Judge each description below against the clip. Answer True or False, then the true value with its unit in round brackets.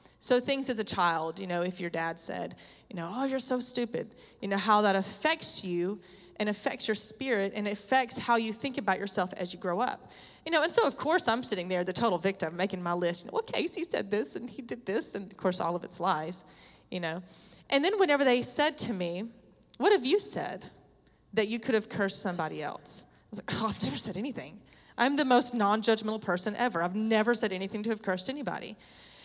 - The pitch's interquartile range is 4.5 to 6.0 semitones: True (5.3 semitones)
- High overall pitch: True (210 Hz)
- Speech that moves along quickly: True (230 wpm)